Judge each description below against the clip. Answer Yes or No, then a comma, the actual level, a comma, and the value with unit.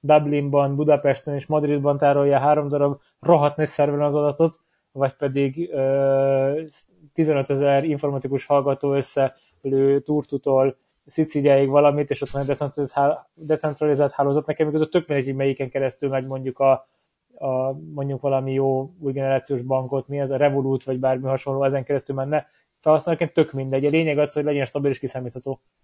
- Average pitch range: No, narrow, 1.6 semitones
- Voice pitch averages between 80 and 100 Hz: No, medium, 140 Hz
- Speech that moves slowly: No, fast, 155 wpm